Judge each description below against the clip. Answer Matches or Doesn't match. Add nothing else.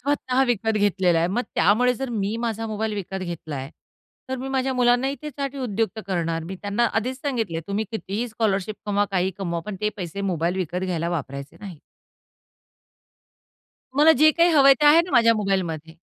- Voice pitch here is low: Doesn't match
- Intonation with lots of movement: Matches